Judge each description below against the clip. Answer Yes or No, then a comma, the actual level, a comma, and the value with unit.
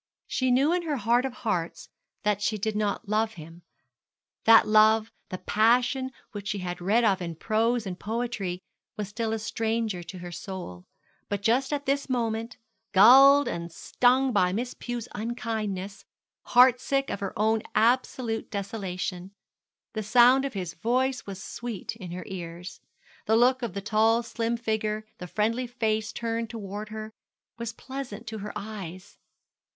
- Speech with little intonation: No, average, 3.3 semitones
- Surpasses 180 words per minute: No, average, 160 wpm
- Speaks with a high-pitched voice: Yes, high, 220 Hz